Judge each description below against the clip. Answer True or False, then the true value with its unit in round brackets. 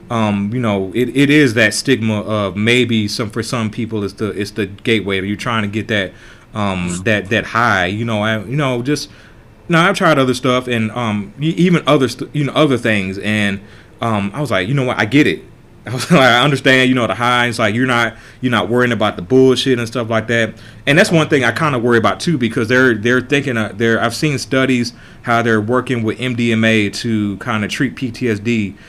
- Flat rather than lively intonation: False (3.2 semitones)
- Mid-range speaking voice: False (115 Hz)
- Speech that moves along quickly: True (230 wpm)